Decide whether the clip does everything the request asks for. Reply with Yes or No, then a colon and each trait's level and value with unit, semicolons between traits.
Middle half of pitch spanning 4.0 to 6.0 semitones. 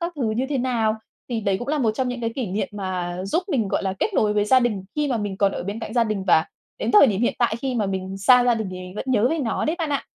Yes: average, 4.5 semitones